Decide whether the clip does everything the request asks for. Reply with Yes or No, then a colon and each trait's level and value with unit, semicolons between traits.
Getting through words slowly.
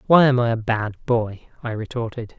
No: average, 200 wpm